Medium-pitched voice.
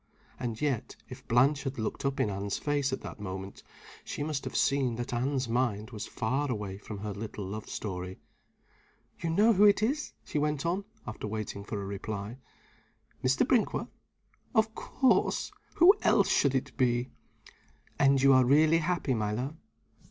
No: low, 130 Hz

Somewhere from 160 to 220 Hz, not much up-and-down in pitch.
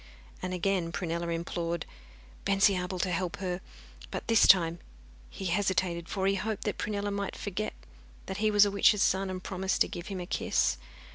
Yes: high, 190 Hz; narrow, 2.3 semitones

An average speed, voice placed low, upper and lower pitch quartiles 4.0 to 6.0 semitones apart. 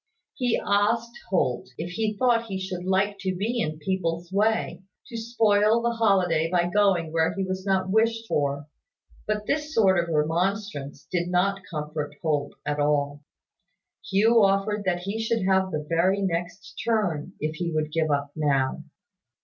No: average, 165 wpm; medium, 185 Hz; average, 4.7 semitones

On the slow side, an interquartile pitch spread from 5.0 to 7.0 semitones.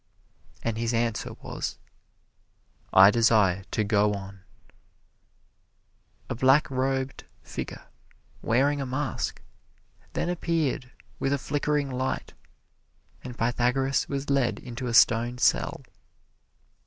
No: slow, 105 wpm; average, 3.0 semitones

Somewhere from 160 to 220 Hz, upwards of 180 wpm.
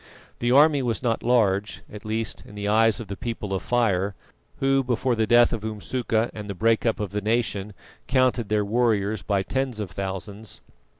No: low, 110 Hz; average, 190 wpm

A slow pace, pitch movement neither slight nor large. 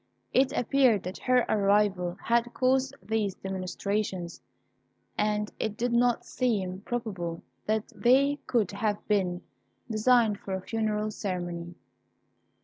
Yes: slow, 120 wpm; average, 4.0 semitones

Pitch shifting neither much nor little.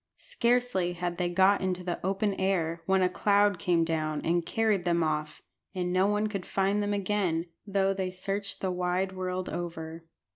No: narrow, 2.3 semitones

